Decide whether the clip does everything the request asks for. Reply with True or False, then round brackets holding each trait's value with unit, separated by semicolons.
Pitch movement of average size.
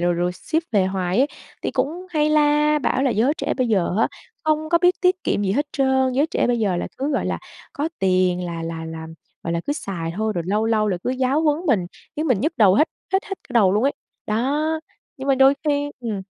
False (7.7 semitones)